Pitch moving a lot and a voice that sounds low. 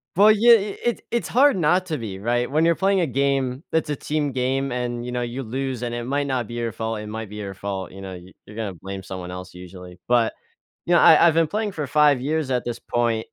Yes: wide, 6.0 semitones; low, 125 Hz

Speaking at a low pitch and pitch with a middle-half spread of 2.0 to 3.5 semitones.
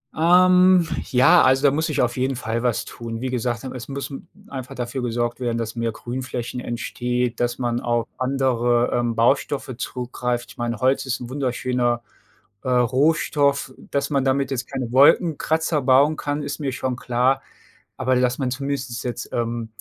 Yes: low, 125 Hz; narrow, 2.5 semitones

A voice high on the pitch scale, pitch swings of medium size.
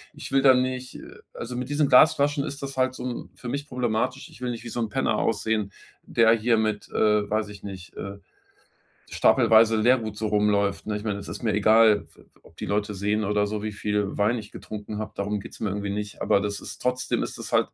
No: low, 110 Hz; average, 3.4 semitones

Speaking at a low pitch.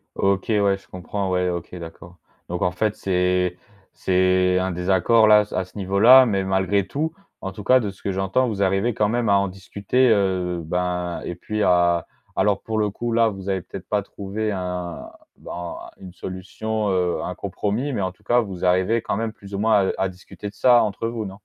Yes: very low, 95 Hz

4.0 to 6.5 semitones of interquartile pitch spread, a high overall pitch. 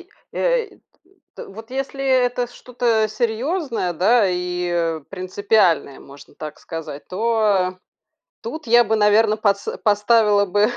Yes: average, 4.7 semitones; high, 215 Hz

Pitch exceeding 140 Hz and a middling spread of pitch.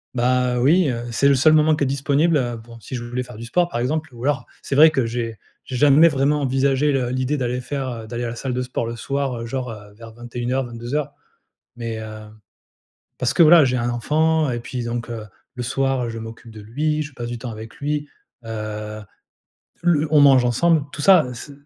No: low, 125 Hz; average, 3.6 semitones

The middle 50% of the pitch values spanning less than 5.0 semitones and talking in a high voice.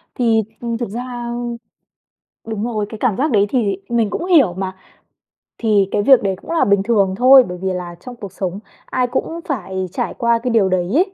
Yes: average, 4.3 semitones; high, 225 Hz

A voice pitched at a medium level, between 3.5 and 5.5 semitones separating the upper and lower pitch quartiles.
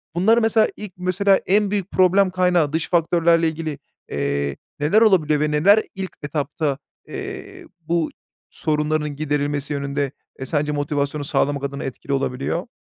Yes: medium, 155 Hz; average, 4.1 semitones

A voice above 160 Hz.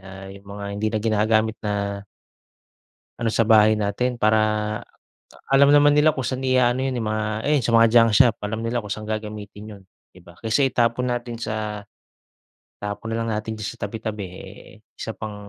No: low, 110 Hz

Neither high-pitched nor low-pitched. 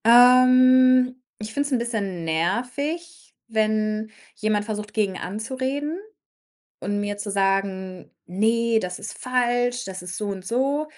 No: high, 220 Hz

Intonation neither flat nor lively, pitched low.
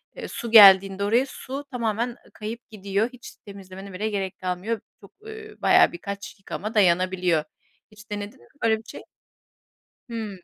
No: average, 3.0 semitones; high, 205 Hz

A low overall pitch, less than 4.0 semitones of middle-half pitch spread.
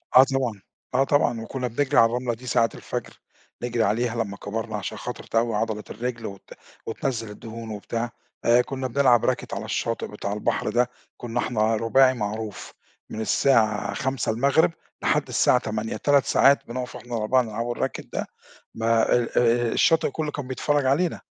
Yes: low, 120 Hz; average, 2.7 semitones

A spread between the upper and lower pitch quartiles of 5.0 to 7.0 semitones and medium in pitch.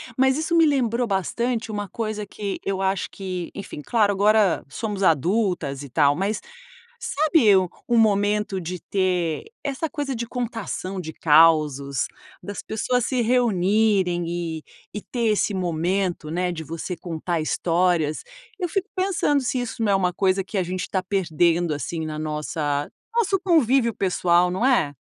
No: average, 5.3 semitones; high, 195 Hz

